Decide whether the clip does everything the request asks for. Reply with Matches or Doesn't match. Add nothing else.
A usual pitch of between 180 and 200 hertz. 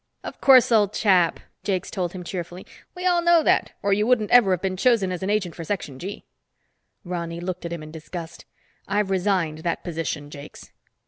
Matches